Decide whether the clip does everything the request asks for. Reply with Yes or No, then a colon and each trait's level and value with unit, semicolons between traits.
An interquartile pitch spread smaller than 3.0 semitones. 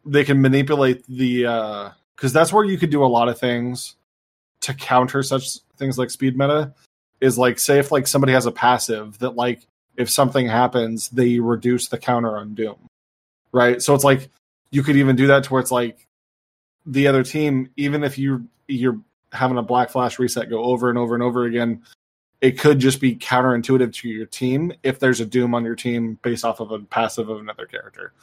Yes: narrow, 2.4 semitones